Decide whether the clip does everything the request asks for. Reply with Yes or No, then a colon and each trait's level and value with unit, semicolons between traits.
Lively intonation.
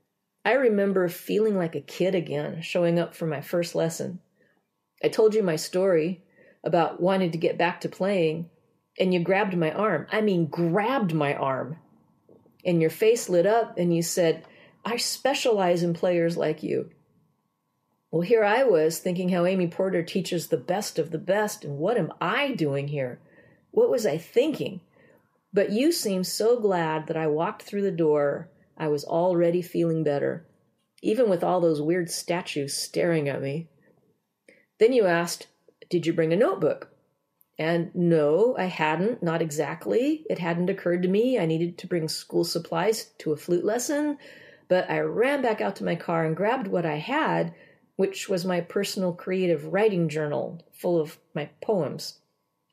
No: average, 3.3 semitones